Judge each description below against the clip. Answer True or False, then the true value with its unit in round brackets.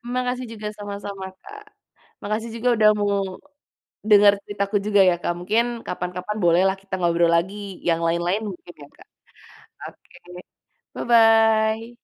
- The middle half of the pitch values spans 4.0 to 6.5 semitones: False (3.6 semitones)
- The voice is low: False (205 Hz)